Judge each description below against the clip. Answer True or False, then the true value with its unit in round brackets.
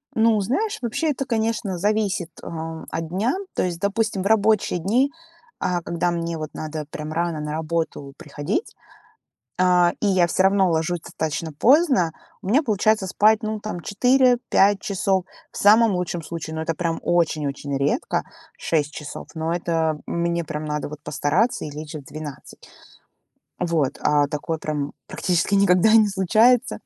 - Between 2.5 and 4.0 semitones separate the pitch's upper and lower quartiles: False (5.3 semitones)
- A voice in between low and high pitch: True (175 Hz)